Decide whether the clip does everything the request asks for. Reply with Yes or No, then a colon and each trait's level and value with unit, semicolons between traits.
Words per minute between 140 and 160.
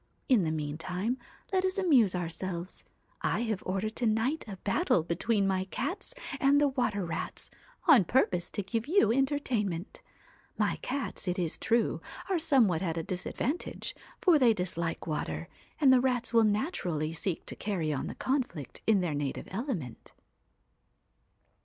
Yes: average, 155 wpm